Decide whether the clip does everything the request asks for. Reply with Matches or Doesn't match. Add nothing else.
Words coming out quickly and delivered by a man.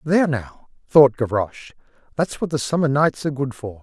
Doesn't match